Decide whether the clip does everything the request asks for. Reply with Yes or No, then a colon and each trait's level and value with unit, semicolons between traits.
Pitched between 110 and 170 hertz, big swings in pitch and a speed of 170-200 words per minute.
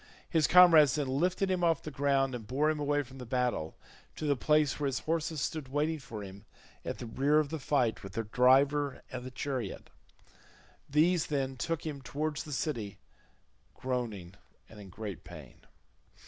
No: medium, 140 Hz; average, 3.7 semitones; average, 180 wpm